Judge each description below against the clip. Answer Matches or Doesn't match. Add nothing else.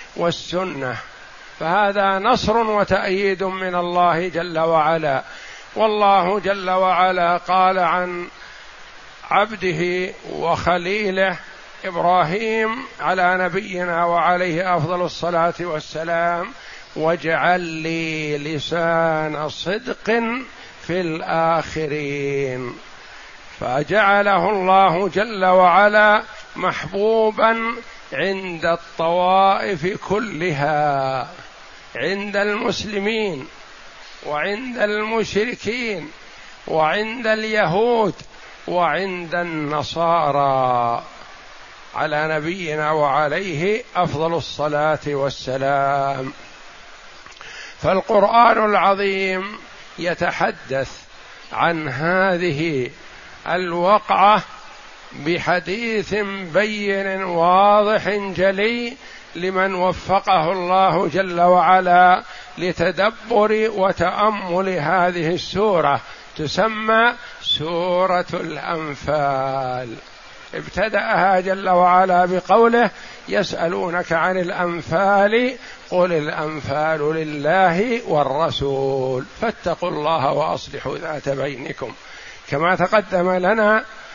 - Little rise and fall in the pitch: Doesn't match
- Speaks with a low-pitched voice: Doesn't match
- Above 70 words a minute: Doesn't match